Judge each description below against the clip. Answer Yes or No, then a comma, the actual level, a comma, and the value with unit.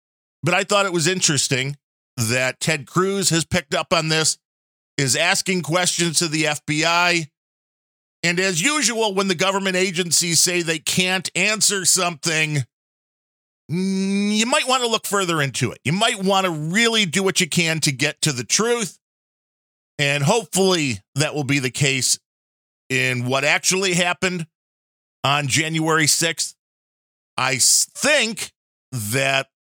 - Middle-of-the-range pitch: Yes, medium, 165 Hz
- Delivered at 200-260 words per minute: No, average, 145 wpm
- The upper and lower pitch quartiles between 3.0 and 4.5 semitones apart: No, average, 5.2 semitones